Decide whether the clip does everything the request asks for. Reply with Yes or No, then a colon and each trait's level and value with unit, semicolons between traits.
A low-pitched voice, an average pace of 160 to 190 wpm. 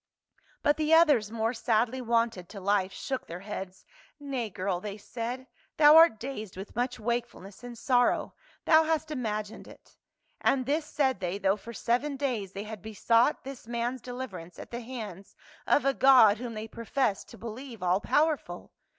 No: high, 235 Hz; average, 170 wpm